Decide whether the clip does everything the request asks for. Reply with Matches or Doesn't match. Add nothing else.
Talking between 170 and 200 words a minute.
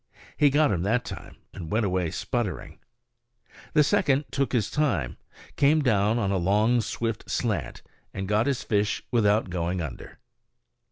Doesn't match